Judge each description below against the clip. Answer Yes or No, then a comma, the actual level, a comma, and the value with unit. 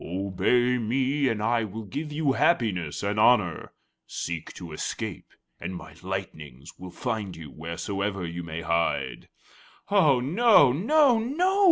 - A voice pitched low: Yes, low, 105 Hz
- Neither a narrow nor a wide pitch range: No, wide, 7.9 semitones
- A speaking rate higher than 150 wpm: No, average, 140 wpm